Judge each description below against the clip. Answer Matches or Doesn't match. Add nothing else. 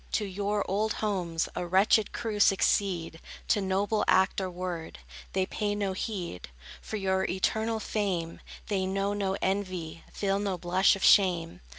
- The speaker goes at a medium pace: Matches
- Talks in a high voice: Matches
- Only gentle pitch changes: Matches